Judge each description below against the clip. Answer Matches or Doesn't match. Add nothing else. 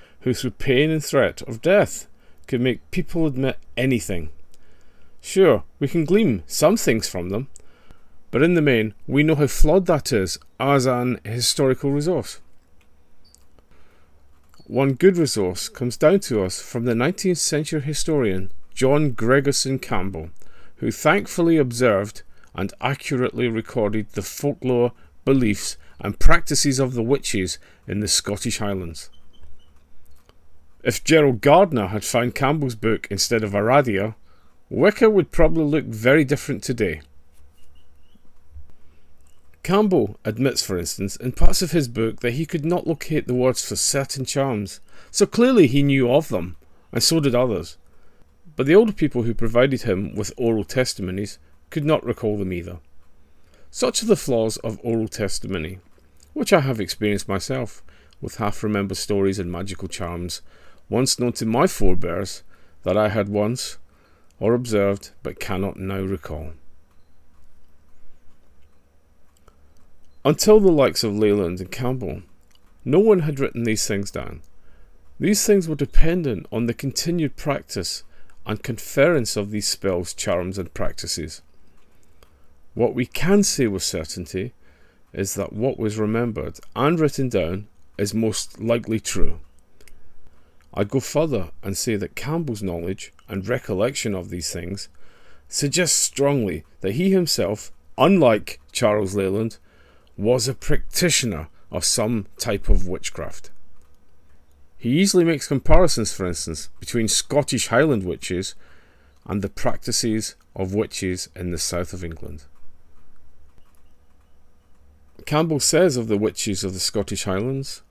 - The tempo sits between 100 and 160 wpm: Matches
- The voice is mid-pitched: Doesn't match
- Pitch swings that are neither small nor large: Doesn't match